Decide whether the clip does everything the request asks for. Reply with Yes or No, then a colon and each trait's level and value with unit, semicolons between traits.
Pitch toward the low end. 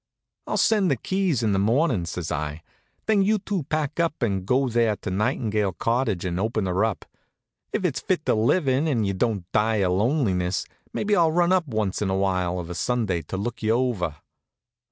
Yes: low, 110 Hz